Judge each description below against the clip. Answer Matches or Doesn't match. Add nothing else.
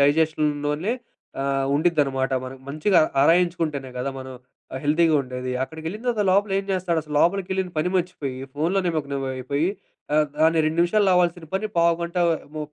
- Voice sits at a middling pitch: Matches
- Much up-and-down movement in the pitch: Doesn't match